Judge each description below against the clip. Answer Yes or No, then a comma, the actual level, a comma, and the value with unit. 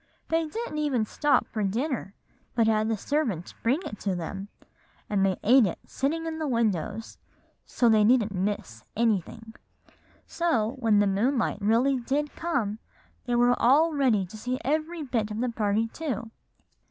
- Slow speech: No, average, 165 wpm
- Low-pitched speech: No, high, 230 Hz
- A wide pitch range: No, average, 5.0 semitones